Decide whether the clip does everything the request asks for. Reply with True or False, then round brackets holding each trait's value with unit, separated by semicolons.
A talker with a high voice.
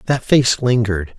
False (115 Hz)